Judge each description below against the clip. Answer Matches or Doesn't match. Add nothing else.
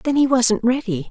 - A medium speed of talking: Doesn't match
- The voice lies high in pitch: Matches